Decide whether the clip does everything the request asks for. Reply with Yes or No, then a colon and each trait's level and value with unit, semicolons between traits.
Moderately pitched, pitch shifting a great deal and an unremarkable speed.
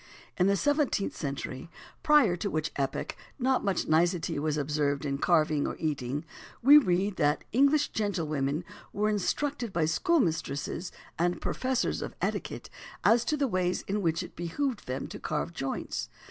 Yes: medium, 175 Hz; wide, 7.0 semitones; average, 155 wpm